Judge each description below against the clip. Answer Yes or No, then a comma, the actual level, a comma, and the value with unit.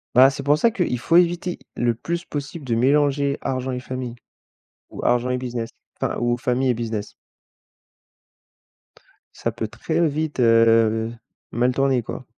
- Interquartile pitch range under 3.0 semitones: No, average, 3.5 semitones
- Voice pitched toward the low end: Yes, low, 130 Hz